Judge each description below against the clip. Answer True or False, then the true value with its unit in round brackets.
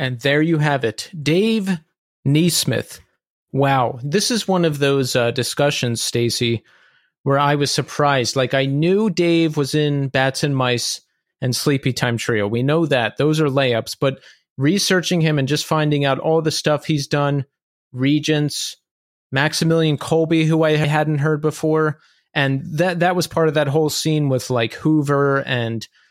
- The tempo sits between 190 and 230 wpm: False (160 wpm)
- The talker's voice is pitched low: False (145 Hz)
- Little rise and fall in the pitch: False (3.0 semitones)